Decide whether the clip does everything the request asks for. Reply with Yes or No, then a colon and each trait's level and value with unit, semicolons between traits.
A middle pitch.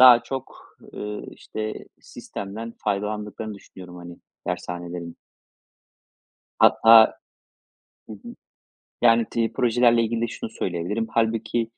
No: low, 110 Hz